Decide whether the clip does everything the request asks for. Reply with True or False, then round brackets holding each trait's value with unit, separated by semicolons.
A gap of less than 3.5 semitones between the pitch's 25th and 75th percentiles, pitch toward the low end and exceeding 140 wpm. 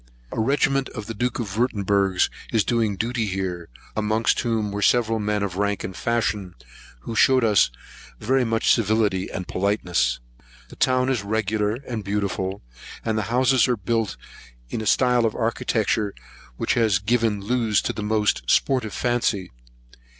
True (2.7 semitones; 110 Hz; 155 wpm)